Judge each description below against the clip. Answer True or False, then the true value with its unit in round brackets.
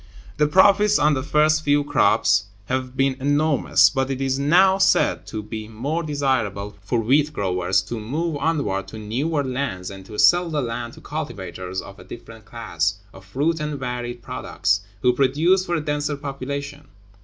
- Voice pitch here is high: False (135 Hz)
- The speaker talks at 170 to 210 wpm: True (175 wpm)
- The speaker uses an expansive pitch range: True (5.7 semitones)